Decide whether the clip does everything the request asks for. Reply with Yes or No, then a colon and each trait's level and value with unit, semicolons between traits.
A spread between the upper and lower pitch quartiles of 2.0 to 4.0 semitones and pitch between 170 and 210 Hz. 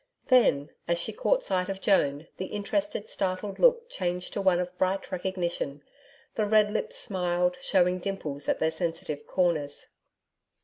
Yes: average, 3.0 semitones; medium, 185 Hz